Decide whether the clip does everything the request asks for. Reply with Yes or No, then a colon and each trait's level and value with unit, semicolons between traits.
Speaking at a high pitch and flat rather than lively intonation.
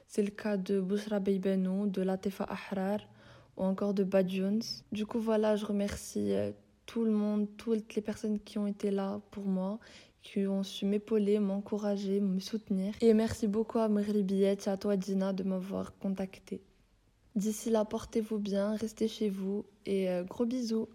Yes: high, 205 Hz; narrow, 1.7 semitones